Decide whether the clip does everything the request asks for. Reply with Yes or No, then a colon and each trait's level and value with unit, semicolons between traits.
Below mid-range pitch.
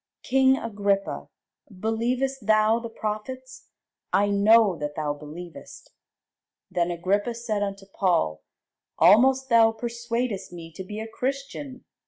No: high, 215 Hz